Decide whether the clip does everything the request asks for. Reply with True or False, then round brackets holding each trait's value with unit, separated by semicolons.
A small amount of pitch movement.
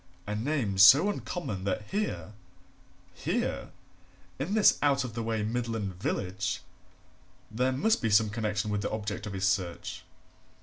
False (4.4 semitones)